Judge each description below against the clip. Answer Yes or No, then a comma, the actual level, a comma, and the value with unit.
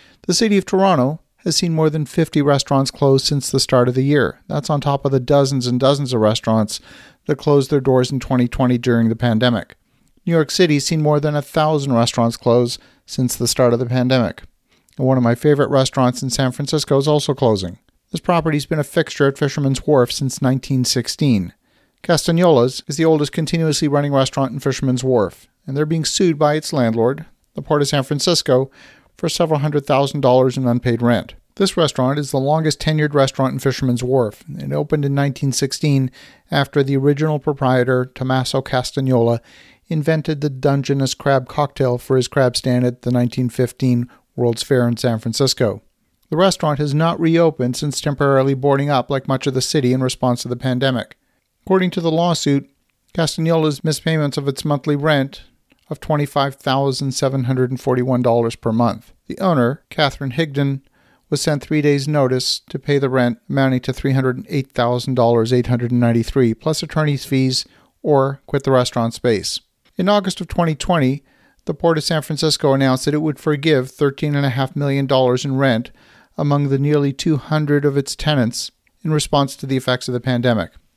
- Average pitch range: Yes, average, 3.0 semitones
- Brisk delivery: No, average, 190 wpm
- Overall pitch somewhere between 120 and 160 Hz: Yes, low, 135 Hz